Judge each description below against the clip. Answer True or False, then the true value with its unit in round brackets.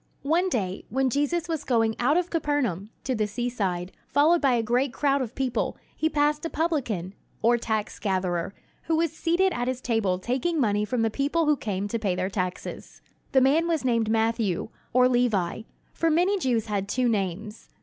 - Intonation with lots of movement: True (5.9 semitones)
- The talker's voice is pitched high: True (245 Hz)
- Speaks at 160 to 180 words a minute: False (190 wpm)